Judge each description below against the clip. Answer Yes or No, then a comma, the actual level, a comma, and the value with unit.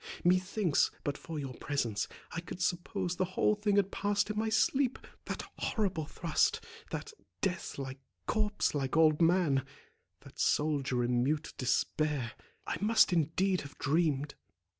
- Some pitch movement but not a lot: No, wide, 5.7 semitones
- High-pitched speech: No, medium, 165 Hz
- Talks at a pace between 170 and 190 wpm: No, slow, 135 wpm